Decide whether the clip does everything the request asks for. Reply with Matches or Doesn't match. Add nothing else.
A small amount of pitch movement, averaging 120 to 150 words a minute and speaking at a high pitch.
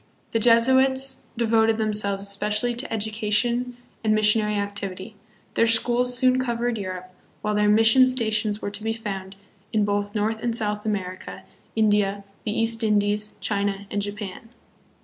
Matches